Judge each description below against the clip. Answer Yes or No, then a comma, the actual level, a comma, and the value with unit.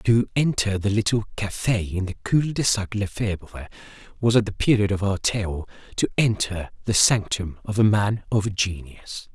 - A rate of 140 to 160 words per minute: No, average, 180 wpm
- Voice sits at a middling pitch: No, low, 100 Hz